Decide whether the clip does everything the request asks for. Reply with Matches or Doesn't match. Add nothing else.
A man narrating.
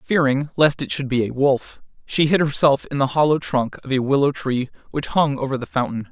Matches